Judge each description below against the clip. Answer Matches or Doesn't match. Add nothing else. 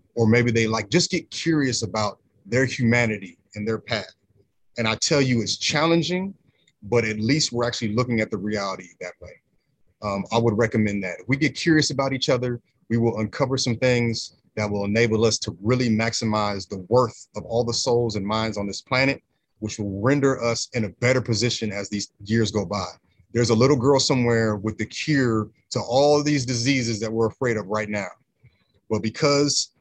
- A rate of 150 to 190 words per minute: Doesn't match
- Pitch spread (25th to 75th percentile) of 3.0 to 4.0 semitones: Matches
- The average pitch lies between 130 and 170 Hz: Doesn't match